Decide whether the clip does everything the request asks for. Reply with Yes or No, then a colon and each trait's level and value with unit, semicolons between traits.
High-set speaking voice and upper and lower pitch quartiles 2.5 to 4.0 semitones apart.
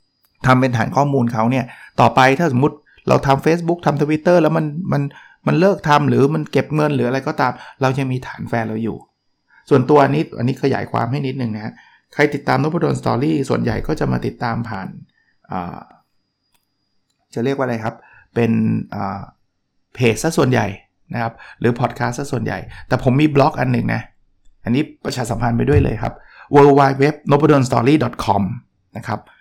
No: low, 135 Hz; average, 3.3 semitones